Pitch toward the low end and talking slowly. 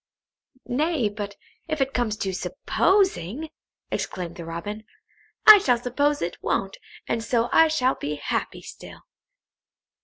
No: high, 240 Hz; slow, 130 wpm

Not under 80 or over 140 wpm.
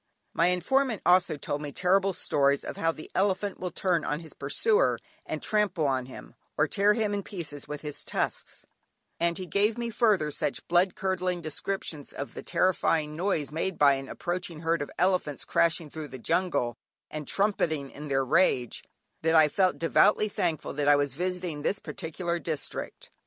No: average, 180 wpm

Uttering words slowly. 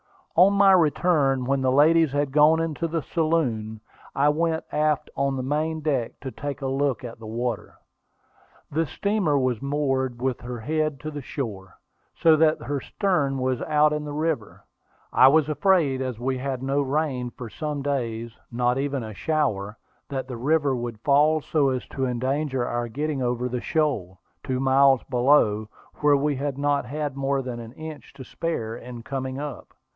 No: average, 185 wpm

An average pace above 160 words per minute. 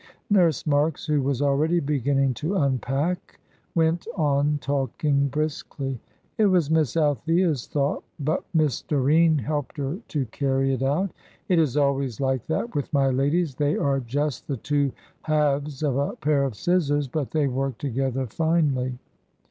No: average, 155 wpm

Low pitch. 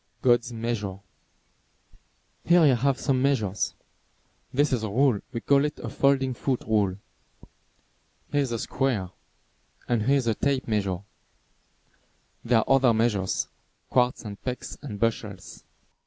Yes: low, 120 Hz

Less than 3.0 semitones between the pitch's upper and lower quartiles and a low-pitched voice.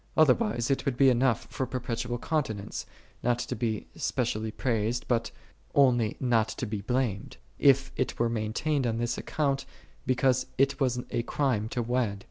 Yes: narrow, 2.5 semitones; low, 120 Hz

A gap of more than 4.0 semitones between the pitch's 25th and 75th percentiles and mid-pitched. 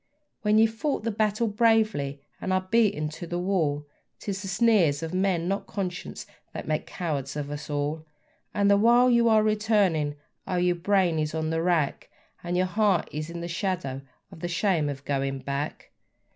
Yes: average, 5.3 semitones; medium, 180 Hz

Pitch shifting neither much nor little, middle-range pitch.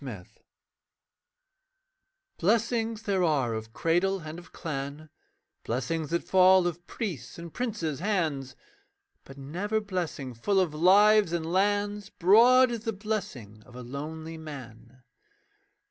No: wide, 6.5 semitones; medium, 170 Hz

